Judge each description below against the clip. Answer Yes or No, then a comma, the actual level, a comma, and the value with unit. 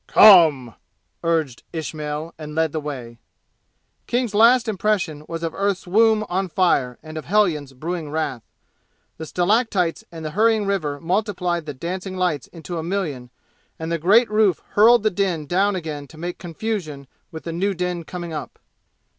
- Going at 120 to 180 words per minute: Yes, average, 165 wpm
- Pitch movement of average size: Yes, average, 4.3 semitones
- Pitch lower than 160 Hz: No, medium, 170 Hz